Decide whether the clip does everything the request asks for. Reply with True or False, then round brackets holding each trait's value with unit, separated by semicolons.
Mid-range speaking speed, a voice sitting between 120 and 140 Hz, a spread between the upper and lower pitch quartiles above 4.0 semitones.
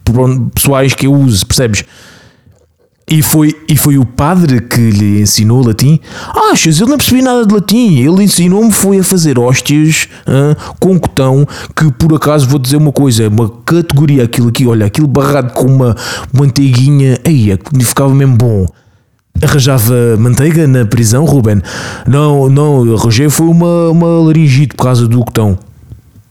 True (160 wpm; 135 Hz; 4.5 semitones)